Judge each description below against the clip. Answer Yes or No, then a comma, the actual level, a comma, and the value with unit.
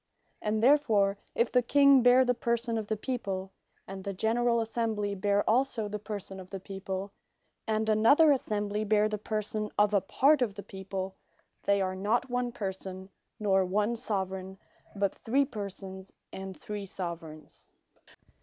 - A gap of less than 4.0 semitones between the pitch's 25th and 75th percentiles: Yes, average, 3.2 semitones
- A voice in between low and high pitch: No, high, 210 Hz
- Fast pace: No, average, 155 wpm